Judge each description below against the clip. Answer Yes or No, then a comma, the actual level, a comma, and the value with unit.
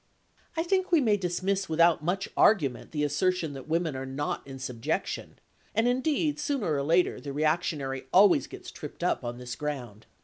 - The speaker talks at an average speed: Yes, average, 175 wpm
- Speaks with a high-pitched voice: No, medium, 160 Hz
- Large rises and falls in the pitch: Yes, wide, 6.3 semitones